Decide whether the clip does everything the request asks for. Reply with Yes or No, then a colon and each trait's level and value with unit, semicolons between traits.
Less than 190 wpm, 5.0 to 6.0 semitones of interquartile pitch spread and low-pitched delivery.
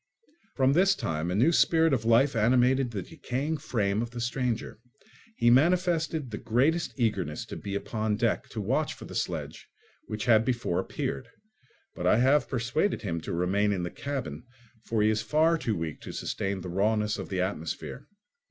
Yes: average, 180 wpm; average, 5.3 semitones; low, 115 Hz